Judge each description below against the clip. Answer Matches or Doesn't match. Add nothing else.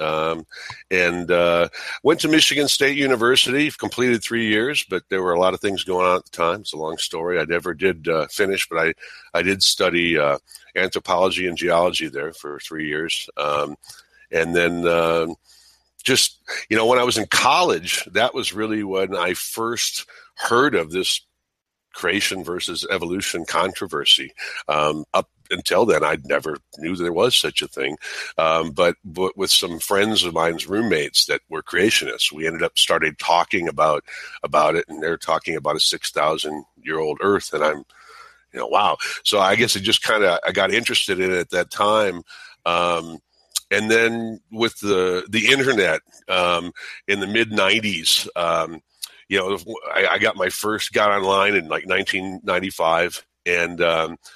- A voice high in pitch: Doesn't match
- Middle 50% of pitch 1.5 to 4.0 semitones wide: Doesn't match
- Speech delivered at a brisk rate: Doesn't match